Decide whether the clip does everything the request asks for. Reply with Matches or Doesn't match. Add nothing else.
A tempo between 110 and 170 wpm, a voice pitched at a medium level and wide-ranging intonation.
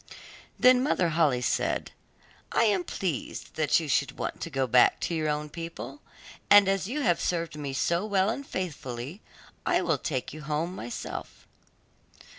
Doesn't match